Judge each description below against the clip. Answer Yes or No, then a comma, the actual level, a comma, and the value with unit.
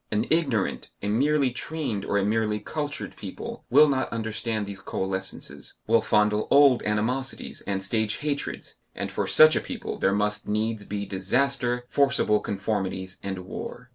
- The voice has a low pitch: Yes, low, 110 Hz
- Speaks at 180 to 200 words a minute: No, average, 155 wpm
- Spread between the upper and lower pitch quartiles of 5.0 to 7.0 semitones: No, average, 4.6 semitones